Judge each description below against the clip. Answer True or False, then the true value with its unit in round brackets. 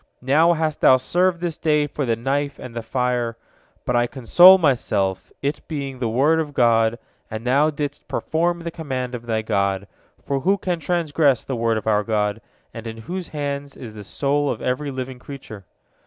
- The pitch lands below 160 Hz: True (135 Hz)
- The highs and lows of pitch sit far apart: False (4.6 semitones)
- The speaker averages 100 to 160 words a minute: False (185 wpm)